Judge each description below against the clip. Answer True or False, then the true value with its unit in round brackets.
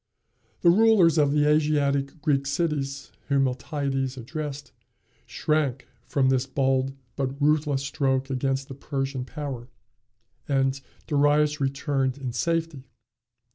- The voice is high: False (140 Hz)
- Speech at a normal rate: False (115 wpm)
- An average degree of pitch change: False (1.9 semitones)